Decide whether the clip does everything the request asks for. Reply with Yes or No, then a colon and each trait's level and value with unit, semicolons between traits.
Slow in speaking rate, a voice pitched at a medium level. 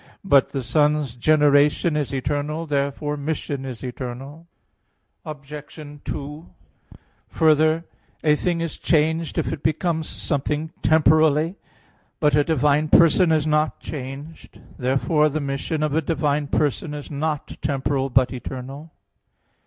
Yes: slow, 125 wpm; medium, 150 Hz